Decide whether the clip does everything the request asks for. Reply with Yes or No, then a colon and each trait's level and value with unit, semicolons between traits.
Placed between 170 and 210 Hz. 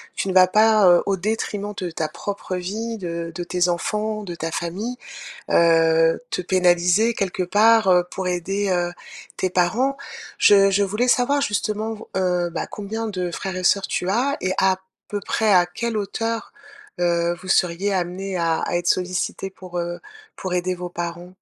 Yes: medium, 185 Hz